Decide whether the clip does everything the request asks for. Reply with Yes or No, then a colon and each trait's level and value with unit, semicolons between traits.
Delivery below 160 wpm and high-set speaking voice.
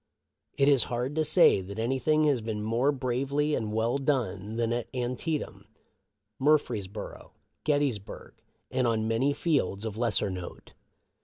No: average, 140 wpm; low, 120 Hz